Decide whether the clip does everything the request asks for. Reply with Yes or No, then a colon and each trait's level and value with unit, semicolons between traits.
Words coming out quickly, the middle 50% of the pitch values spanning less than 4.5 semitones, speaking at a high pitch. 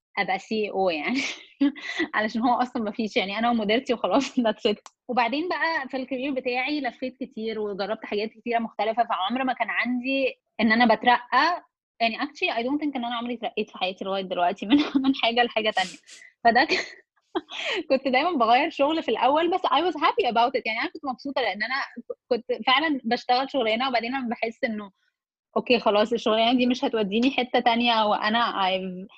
Yes: fast, 180 wpm; average, 3.5 semitones; high, 245 Hz